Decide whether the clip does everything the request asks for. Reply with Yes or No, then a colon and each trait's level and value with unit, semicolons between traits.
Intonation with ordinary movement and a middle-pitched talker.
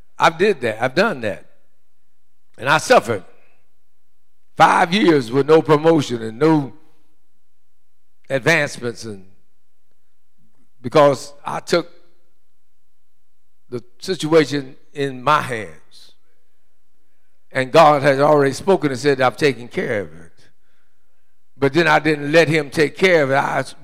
Yes: average, 3.2 semitones; medium, 145 Hz